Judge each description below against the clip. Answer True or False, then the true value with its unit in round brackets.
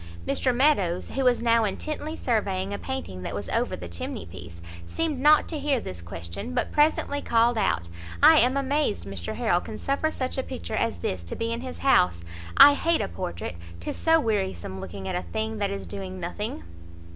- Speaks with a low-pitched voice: False (215 Hz)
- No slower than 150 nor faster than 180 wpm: False (200 wpm)